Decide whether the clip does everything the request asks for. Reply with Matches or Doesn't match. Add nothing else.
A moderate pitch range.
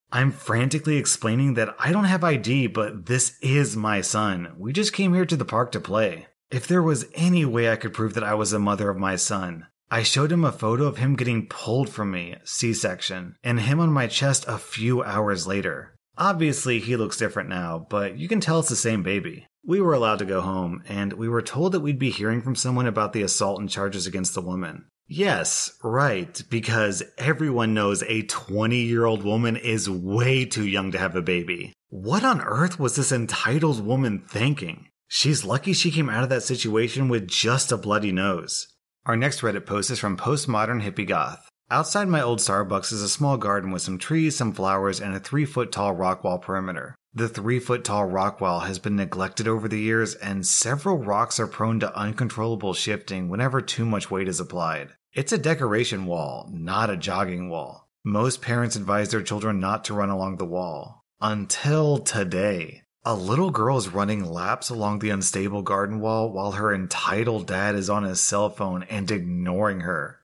Matches